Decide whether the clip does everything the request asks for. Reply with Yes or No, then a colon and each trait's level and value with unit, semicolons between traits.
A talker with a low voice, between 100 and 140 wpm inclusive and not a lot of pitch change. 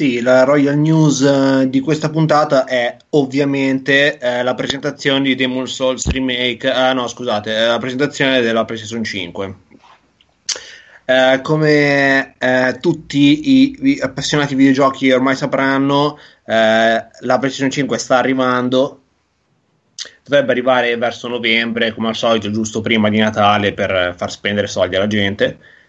No: low, 130 Hz; average, 130 wpm; average, 3.1 semitones